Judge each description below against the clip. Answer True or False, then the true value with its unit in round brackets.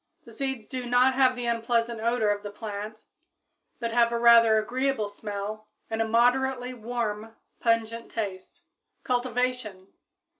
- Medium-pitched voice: False (230 Hz)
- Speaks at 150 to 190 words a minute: False (140 wpm)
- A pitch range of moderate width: False (2.3 semitones)